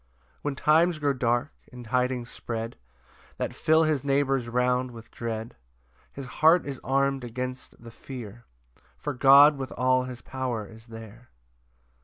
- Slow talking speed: No, average, 150 wpm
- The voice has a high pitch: No, low, 125 Hz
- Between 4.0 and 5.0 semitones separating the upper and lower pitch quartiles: No, narrow, 2.6 semitones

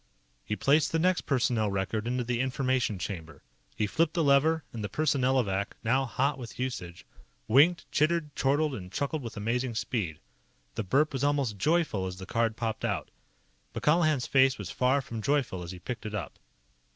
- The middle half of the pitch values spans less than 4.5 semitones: No, average, 5.2 semitones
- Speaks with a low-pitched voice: Yes, low, 125 Hz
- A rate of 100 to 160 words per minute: No, average, 180 wpm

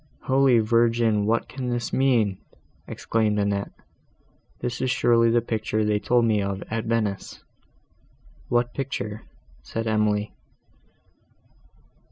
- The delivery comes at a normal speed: No, slow, 115 wpm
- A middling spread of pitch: No, narrow, 2.2 semitones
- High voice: No, low, 115 Hz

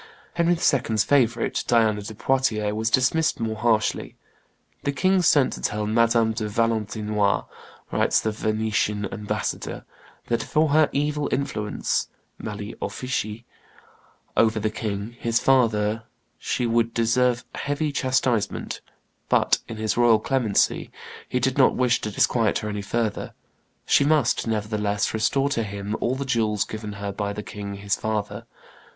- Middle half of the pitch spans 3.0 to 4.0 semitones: Yes, average, 3.3 semitones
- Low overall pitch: Yes, low, 110 Hz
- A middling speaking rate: Yes, average, 145 wpm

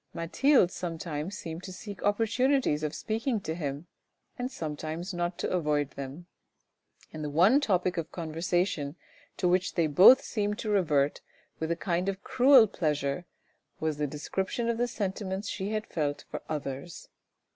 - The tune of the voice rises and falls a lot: No, average, 4.9 semitones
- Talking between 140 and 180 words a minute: Yes, average, 155 wpm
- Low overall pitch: No, medium, 175 Hz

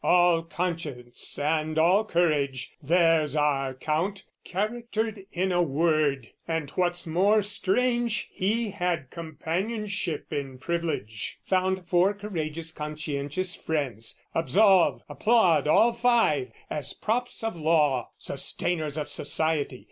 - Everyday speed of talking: No, slow, 110 wpm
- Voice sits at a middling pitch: Yes, medium, 165 Hz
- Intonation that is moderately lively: Yes, average, 4.4 semitones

